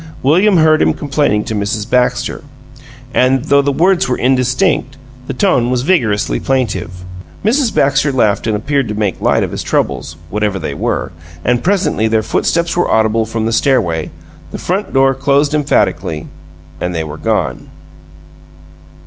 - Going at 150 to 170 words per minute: Yes, average, 155 wpm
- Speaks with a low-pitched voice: Yes, low, 125 Hz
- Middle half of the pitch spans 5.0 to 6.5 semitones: Yes, average, 5.3 semitones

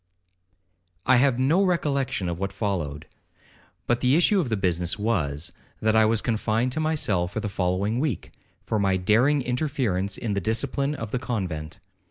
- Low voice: Yes, low, 110 Hz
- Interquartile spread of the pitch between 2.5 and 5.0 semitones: No, wide, 5.6 semitones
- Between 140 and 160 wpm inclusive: No, average, 175 wpm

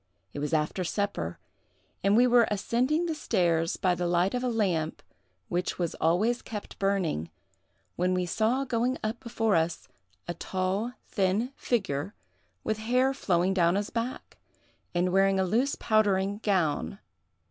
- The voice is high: Yes, high, 195 Hz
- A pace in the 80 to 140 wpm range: No, average, 150 wpm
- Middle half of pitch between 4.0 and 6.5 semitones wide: Yes, average, 4.7 semitones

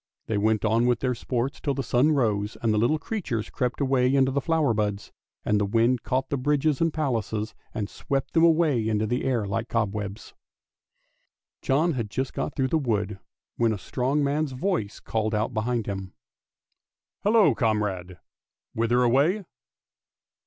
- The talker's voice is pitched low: Yes, low, 120 Hz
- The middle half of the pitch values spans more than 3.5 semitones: Yes, average, 4.4 semitones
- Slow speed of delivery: No, average, 170 wpm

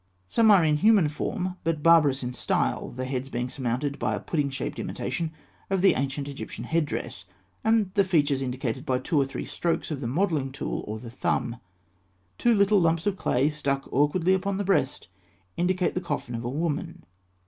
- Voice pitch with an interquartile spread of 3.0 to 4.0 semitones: No, wide, 5.5 semitones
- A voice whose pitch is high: No, medium, 150 Hz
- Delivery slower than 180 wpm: No, average, 190 wpm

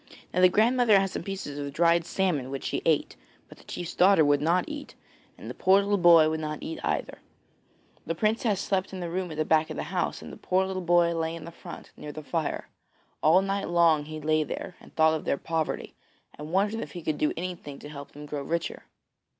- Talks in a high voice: No, medium, 170 Hz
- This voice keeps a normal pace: No, fast, 235 wpm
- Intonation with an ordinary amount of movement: Yes, average, 3.4 semitones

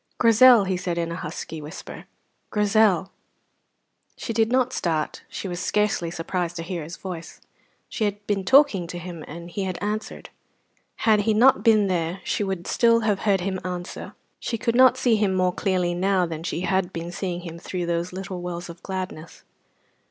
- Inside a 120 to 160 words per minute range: No, average, 185 wpm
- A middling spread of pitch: Yes, average, 3.4 semitones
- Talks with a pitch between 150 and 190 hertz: Yes, medium, 185 Hz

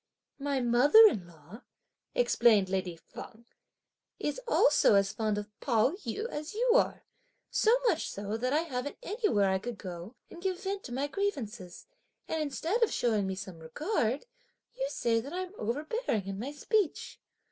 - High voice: Yes, very high, 250 Hz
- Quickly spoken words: No, average, 165 wpm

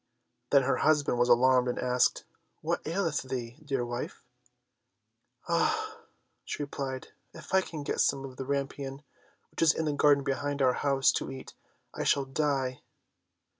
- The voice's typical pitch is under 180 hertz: Yes, low, 135 Hz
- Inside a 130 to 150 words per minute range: No, average, 160 wpm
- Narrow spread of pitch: Yes, narrow, 2.0 semitones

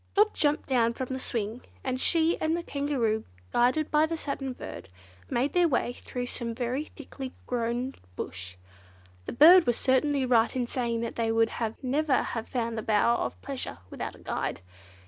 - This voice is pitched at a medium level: No, very high, 255 Hz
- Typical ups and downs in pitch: Yes, average, 3.7 semitones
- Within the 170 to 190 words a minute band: Yes, average, 180 wpm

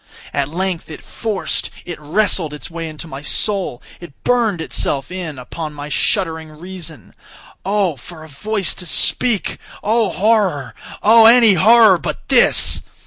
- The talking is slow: Yes, slow, 130 wpm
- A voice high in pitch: No, medium, 175 Hz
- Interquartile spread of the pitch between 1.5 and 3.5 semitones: No, wide, 5.4 semitones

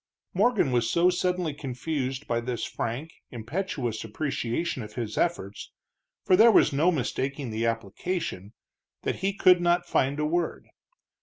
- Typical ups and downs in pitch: No, wide, 6.8 semitones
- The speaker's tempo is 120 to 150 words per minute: Yes, average, 145 wpm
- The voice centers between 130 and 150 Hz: Yes, medium, 140 Hz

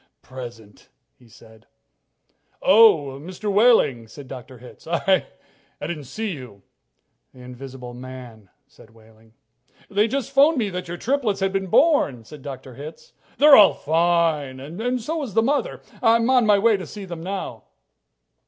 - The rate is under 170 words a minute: Yes, average, 155 wpm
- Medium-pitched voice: Yes, medium, 170 Hz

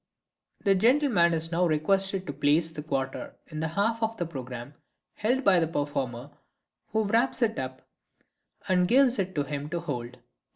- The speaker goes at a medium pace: Yes, average, 170 wpm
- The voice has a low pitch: No, medium, 170 Hz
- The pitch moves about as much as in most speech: No, wide, 5.9 semitones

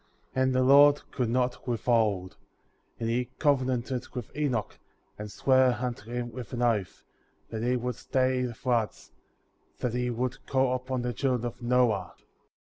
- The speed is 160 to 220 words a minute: Yes, average, 165 wpm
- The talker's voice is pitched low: Yes, low, 125 Hz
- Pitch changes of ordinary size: No, narrow, 1.5 semitones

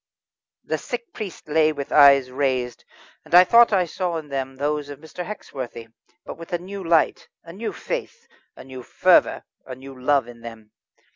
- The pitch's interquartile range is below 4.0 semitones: No, average, 5.3 semitones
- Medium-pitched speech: Yes, medium, 145 Hz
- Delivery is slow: No, average, 185 wpm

